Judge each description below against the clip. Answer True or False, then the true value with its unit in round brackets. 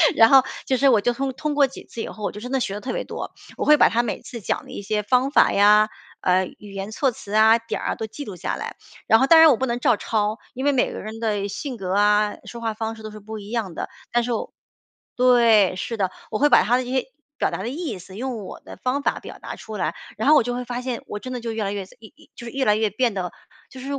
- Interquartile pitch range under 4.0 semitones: True (3.4 semitones)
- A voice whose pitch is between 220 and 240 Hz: True (225 Hz)